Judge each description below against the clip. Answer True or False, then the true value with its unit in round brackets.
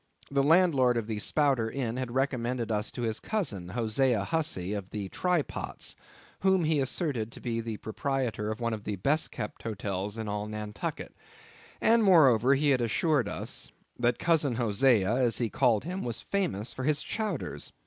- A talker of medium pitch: False (120 Hz)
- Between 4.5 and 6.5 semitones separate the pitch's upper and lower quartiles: True (5.1 semitones)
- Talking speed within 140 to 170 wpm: False (180 wpm)